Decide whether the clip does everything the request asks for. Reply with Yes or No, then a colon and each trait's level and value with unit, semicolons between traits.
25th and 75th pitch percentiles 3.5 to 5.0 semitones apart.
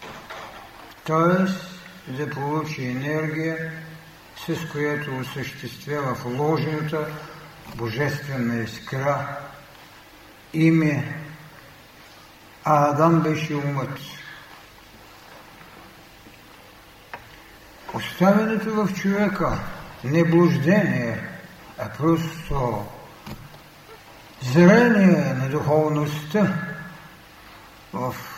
No: average, 2.8 semitones